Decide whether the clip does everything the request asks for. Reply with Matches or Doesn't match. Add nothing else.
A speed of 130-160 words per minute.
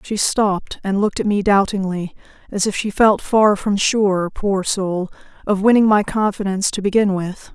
Doesn't match